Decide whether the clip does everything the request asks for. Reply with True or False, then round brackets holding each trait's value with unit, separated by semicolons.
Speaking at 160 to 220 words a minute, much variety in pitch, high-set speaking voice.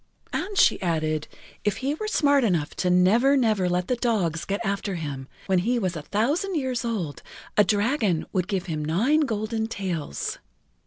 True (175 wpm; 5.7 semitones; 205 Hz)